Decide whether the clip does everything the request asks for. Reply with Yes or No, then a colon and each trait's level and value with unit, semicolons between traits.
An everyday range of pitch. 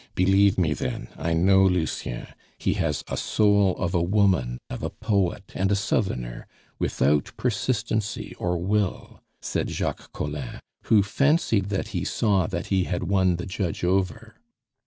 Yes: average, 3.1 semitones